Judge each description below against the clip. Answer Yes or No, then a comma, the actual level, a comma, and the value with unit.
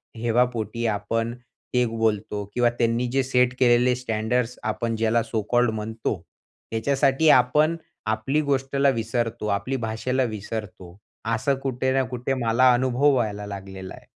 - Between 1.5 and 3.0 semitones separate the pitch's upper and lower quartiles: Yes, narrow, 2.5 semitones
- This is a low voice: Yes, low, 120 Hz